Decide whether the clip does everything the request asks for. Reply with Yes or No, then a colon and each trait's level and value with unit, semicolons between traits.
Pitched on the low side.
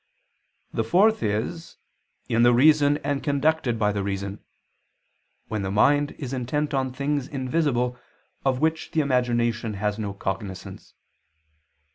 Yes: low, 125 Hz